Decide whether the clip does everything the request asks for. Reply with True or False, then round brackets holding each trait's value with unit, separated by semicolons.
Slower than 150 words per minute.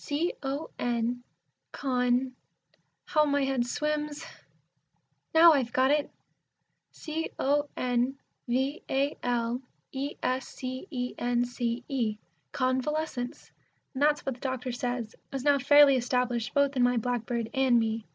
True (140 wpm)